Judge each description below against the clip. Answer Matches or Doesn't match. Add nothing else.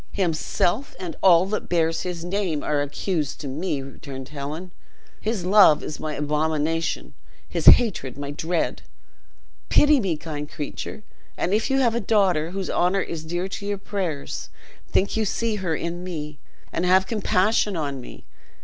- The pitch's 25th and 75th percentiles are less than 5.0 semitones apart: Matches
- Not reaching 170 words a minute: Matches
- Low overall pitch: Doesn't match